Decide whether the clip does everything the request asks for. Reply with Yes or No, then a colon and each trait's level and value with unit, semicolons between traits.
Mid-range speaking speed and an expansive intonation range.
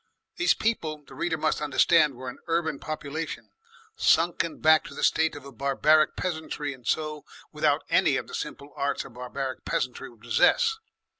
No: average, 170 wpm; average, 2.7 semitones